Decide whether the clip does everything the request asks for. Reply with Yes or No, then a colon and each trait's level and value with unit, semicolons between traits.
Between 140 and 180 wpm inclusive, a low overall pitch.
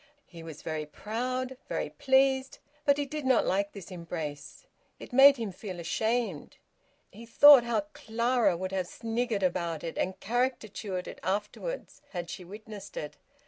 No: average, 155 wpm; high, 210 Hz